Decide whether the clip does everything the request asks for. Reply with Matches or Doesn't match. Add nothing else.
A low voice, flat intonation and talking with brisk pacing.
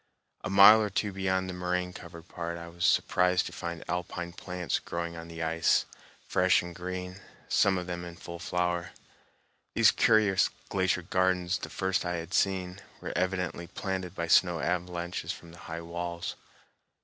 Doesn't match